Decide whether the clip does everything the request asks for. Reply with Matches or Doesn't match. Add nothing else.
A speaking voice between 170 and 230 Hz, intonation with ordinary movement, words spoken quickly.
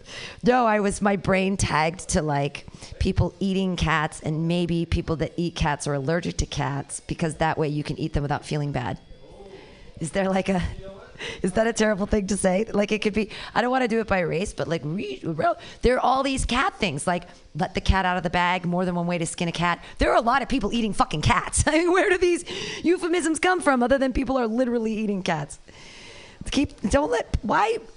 Doesn't match